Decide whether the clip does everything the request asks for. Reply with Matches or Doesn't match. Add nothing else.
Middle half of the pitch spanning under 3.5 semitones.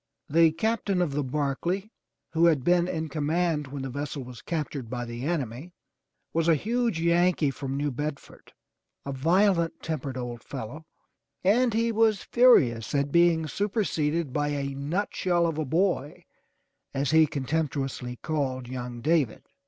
Doesn't match